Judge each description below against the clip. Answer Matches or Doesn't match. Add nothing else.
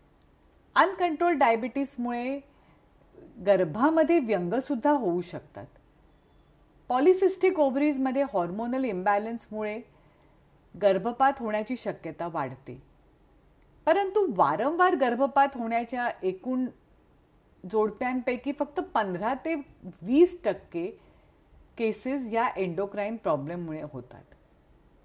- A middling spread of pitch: Doesn't match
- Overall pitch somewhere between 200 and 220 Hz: Doesn't match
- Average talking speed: Doesn't match